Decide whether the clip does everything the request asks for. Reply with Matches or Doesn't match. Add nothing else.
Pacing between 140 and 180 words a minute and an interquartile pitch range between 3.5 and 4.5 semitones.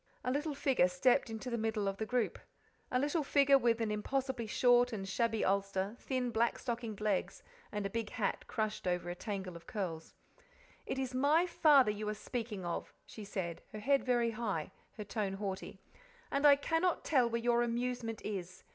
Doesn't match